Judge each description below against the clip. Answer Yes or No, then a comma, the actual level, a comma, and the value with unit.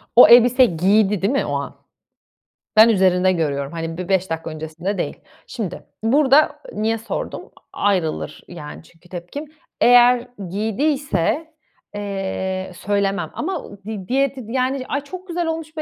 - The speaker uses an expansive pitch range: Yes, wide, 6.4 semitones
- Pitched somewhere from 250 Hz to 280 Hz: No, high, 205 Hz